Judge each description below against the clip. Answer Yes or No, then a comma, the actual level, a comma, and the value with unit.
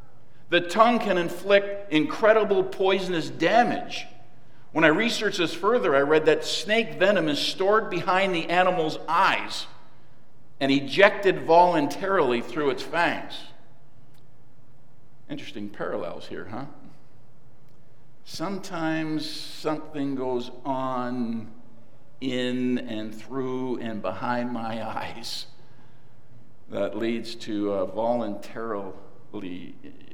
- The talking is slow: Yes, slow, 100 wpm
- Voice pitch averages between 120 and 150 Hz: Yes, medium, 140 Hz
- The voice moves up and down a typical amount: No, wide, 5.9 semitones